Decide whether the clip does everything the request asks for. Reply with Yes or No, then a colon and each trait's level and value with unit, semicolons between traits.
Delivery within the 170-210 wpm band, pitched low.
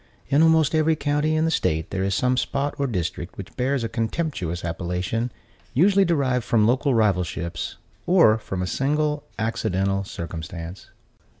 No: average, 155 wpm; low, 115 Hz